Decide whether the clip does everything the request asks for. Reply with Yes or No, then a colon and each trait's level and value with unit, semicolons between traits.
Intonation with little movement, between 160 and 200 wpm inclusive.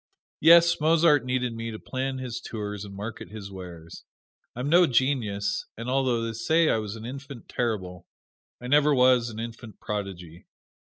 No: average, 4.4 semitones; average, 165 wpm